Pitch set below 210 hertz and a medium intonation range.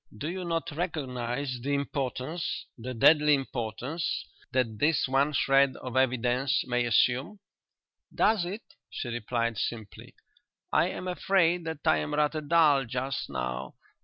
Yes: low, 135 Hz; average, 4.3 semitones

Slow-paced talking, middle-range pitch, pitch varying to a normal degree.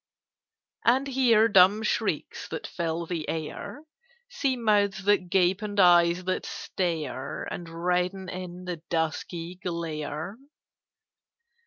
Yes: slow, 115 wpm; medium, 180 Hz; average, 3.3 semitones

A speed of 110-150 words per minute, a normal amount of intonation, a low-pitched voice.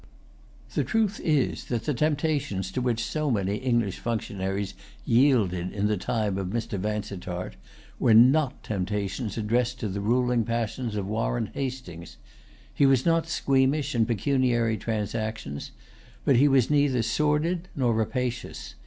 Yes: average, 140 wpm; average, 4.5 semitones; low, 115 Hz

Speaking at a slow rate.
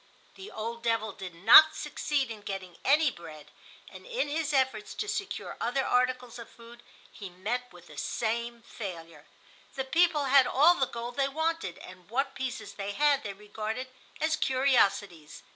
No: average, 165 wpm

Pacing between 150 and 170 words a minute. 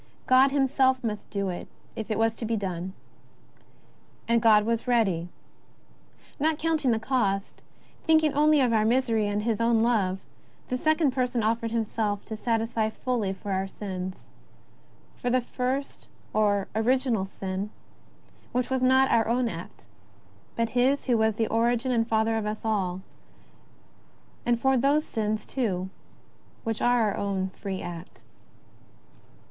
Yes: average, 155 wpm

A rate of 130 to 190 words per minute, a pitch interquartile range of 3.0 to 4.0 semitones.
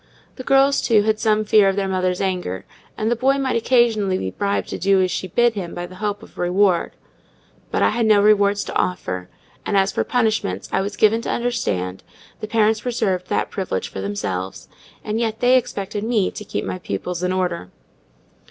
No: average, 200 wpm; average, 3.5 semitones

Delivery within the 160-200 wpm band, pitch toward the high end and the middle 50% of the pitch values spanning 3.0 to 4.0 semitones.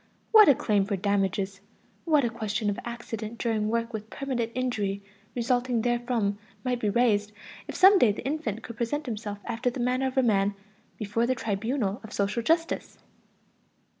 Yes: average, 170 wpm; high, 230 Hz; average, 3.4 semitones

